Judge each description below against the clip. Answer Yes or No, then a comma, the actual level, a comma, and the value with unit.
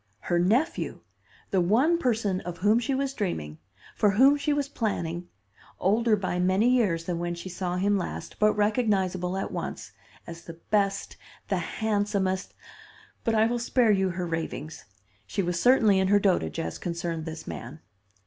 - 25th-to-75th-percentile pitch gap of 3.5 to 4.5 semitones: Yes, average, 4.2 semitones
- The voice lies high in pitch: Yes, high, 195 Hz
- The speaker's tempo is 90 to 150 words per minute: No, average, 170 wpm